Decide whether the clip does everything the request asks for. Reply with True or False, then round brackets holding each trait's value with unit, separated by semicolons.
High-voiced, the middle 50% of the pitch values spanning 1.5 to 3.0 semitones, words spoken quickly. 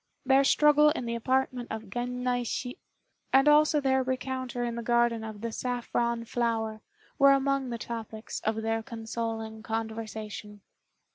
False (235 Hz; 2.7 semitones; 145 wpm)